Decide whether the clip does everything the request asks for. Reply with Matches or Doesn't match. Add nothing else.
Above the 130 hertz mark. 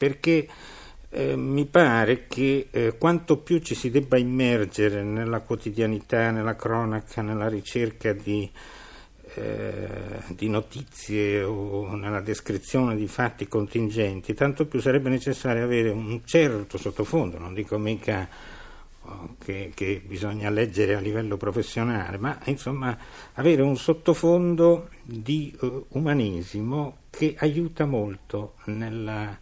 Doesn't match